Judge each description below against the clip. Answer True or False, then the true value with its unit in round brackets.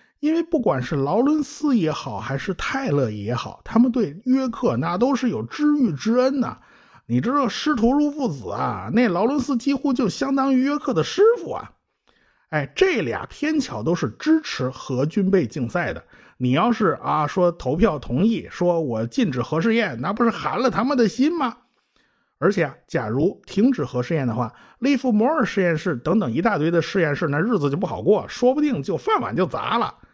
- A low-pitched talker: False (230 Hz)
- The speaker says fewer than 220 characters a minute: False (280 characters per minute)